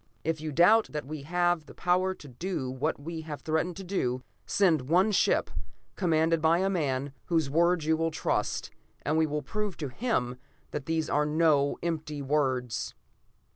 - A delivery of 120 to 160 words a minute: No, average, 175 wpm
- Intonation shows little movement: No, average, 3.3 semitones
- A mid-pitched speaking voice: Yes, medium, 160 Hz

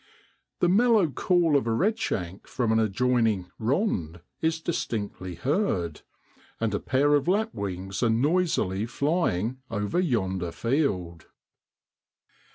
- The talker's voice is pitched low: Yes, low, 115 Hz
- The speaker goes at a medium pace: No, slow, 120 wpm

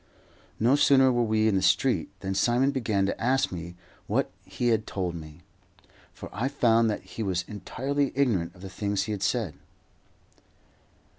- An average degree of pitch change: Yes, average, 4.6 semitones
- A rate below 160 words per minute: No, average, 170 wpm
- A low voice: Yes, low, 110 Hz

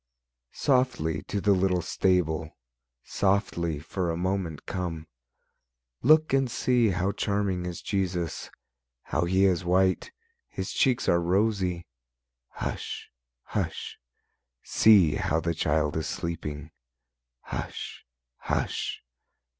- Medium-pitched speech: No, very low, 90 Hz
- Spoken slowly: Yes, slow, 105 wpm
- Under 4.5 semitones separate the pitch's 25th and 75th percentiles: Yes, average, 3.1 semitones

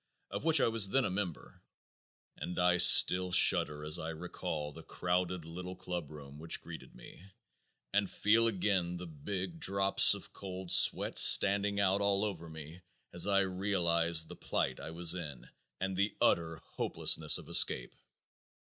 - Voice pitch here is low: Yes, very low, 90 Hz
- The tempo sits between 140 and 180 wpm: Yes, average, 160 wpm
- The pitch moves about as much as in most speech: Yes, average, 3.0 semitones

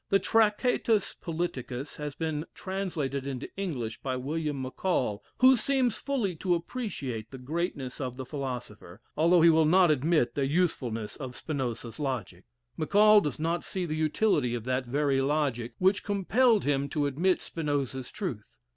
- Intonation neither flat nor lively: No, wide, 5.8 semitones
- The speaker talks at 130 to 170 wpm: Yes, average, 155 wpm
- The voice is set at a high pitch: No, medium, 150 Hz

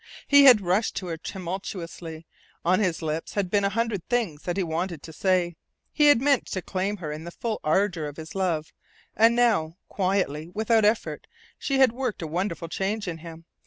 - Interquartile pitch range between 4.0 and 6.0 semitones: Yes, average, 4.7 semitones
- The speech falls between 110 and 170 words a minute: No, average, 200 wpm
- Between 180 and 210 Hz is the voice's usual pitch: Yes, medium, 185 Hz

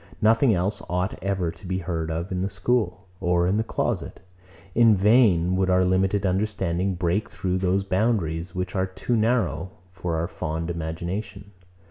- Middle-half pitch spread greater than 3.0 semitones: No, average, 2.7 semitones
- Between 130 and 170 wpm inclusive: Yes, average, 165 wpm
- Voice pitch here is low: Yes, very low, 95 Hz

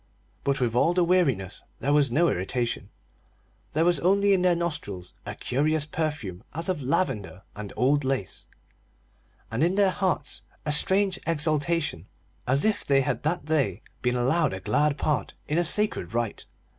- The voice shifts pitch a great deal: Yes, wide, 5.9 semitones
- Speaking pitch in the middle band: Yes, medium, 150 Hz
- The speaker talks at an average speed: Yes, average, 165 wpm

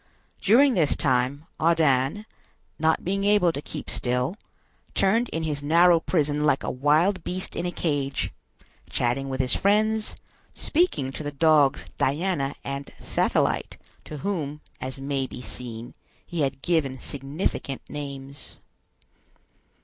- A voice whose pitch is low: No, medium, 145 Hz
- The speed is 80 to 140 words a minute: Yes, slow, 135 wpm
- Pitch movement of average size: Yes, average, 4.4 semitones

